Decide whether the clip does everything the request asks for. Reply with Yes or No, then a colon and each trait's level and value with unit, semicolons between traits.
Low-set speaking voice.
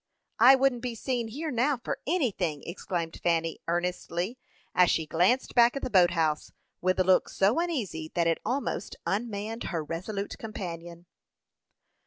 No: high, 195 Hz